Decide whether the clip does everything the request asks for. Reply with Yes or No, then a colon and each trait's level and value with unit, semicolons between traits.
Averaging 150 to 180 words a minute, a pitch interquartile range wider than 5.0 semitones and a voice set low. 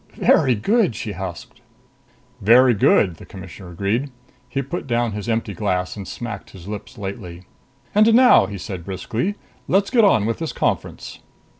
Yes: average, 160 wpm; wide, 5.5 semitones; low, 105 Hz